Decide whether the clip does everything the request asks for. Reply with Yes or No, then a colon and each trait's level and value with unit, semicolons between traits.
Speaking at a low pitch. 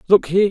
No: high, 190 Hz